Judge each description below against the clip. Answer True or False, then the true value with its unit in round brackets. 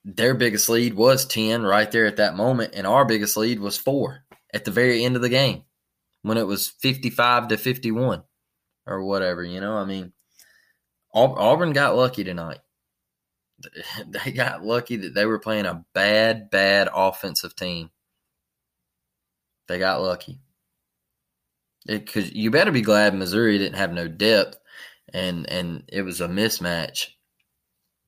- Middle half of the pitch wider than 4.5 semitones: True (5.1 semitones)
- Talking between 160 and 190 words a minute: False (150 wpm)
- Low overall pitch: True (100 Hz)